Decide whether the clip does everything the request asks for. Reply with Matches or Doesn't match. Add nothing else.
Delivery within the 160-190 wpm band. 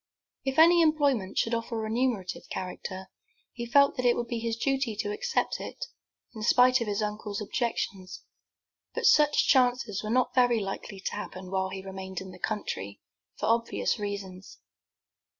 Matches